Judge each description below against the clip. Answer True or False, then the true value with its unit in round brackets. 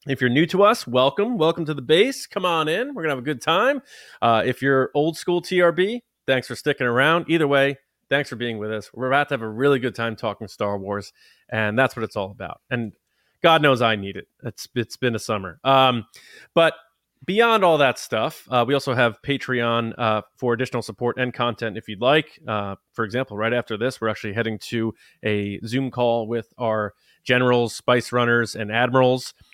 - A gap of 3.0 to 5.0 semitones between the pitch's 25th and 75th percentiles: True (3.9 semitones)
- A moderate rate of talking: False (210 wpm)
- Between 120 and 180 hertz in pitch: True (125 Hz)